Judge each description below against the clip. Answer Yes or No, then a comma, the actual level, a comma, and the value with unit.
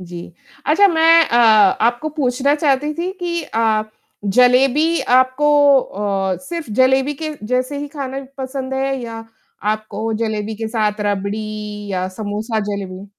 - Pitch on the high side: Yes, very high, 250 Hz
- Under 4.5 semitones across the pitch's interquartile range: No, average, 5.0 semitones